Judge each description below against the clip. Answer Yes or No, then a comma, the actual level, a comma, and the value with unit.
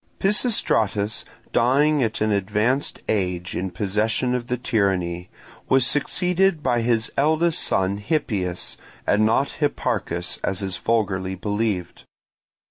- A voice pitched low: Yes, low, 110 Hz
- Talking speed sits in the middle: No, slow, 120 wpm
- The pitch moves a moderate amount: No, wide, 5.7 semitones